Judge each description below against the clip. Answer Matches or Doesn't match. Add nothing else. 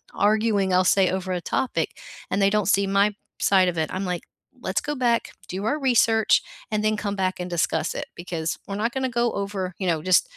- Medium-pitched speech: Doesn't match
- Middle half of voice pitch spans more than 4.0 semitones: Doesn't match